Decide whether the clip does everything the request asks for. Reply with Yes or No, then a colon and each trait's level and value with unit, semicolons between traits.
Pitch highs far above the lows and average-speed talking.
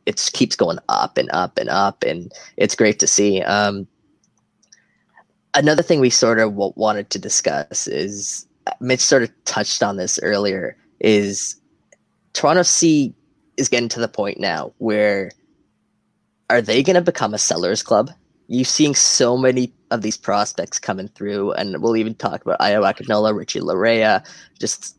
No: average, 3.8 semitones; average, 160 wpm